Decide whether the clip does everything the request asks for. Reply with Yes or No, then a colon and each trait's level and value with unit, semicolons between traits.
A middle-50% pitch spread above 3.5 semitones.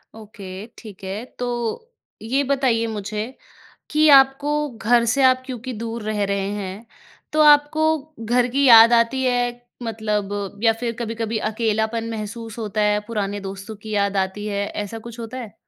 No: average, 2.8 semitones